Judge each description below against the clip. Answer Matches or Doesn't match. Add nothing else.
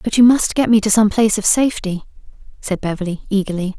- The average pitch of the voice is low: Doesn't match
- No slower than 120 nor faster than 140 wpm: Doesn't match